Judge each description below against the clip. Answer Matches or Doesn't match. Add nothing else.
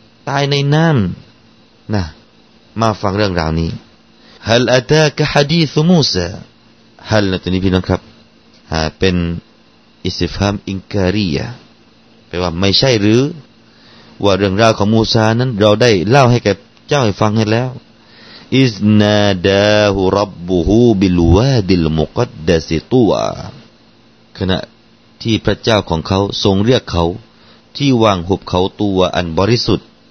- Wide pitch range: Doesn't match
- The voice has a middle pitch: Doesn't match